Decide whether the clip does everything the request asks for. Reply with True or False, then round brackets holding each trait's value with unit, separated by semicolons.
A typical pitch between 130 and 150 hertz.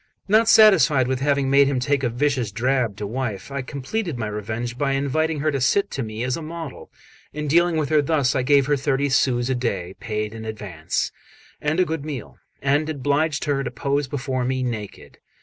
True (135 Hz)